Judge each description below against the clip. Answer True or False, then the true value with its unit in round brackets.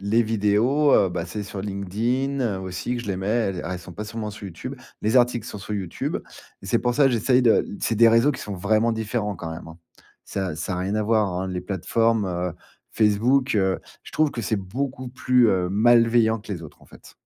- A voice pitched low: True (105 Hz)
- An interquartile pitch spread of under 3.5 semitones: False (3.8 semitones)